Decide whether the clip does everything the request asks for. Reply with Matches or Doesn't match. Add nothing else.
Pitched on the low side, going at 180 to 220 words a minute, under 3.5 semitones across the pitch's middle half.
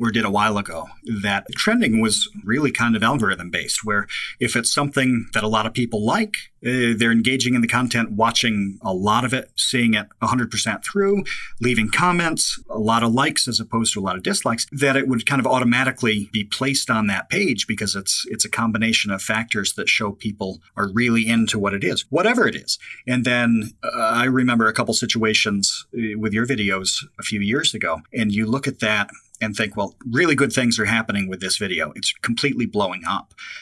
Matches